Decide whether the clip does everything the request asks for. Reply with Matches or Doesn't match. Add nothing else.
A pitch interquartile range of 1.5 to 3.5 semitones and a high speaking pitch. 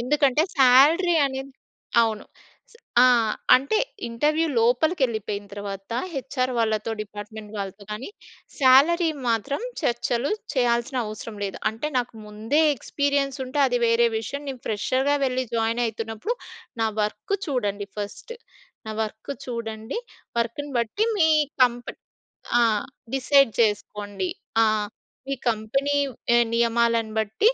Doesn't match